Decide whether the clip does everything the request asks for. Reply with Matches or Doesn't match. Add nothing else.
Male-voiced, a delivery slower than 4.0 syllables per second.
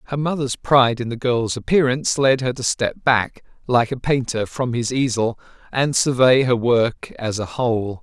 Doesn't match